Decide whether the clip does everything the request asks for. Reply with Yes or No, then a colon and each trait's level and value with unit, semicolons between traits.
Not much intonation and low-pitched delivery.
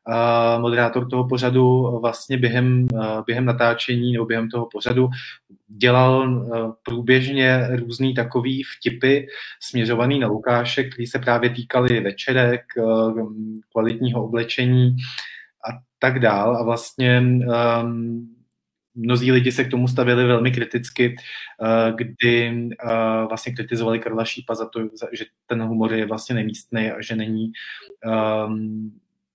Yes: narrow, 1.8 semitones; low, 120 Hz